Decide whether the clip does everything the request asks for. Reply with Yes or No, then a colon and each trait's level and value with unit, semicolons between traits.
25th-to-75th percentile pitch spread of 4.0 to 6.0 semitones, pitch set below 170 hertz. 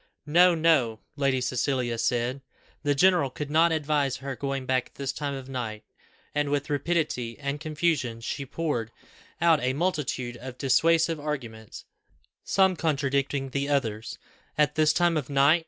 No: average, 3.3 semitones; medium, 140 Hz